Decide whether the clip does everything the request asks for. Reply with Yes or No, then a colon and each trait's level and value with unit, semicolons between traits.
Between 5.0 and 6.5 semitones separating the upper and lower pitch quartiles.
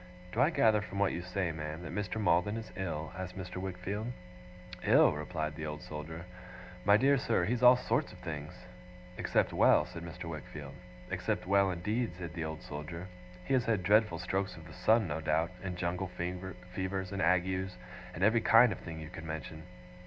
No: average, 3.6 semitones